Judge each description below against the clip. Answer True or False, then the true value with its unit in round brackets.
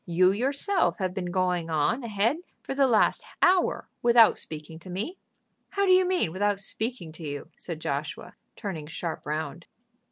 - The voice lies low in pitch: False (190 Hz)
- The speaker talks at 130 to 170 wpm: True (165 wpm)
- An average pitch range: False (6.8 semitones)